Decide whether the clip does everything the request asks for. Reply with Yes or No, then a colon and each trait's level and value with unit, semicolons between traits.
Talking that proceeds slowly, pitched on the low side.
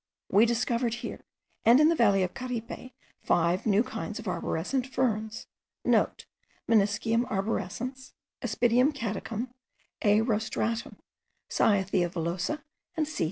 No: slow, 115 wpm; high, 225 Hz